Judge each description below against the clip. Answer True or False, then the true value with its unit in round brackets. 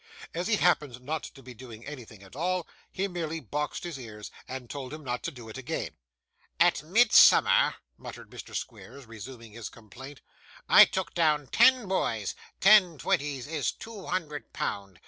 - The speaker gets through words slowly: False (165 wpm)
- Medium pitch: True (145 Hz)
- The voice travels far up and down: True (6.2 semitones)